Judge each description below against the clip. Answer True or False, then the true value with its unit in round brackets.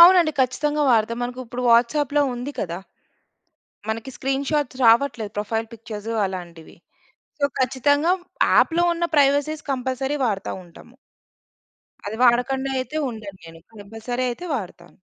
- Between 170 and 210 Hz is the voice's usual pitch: False (250 Hz)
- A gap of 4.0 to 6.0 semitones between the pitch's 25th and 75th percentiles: True (4.5 semitones)